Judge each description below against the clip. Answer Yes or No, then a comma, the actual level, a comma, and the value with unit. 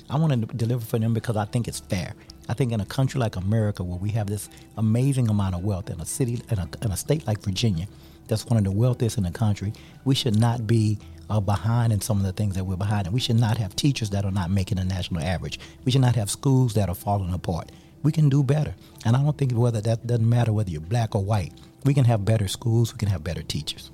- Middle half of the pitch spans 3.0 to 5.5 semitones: Yes, average, 3.4 semitones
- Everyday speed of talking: No, fast, 270 wpm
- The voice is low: Yes, low, 110 Hz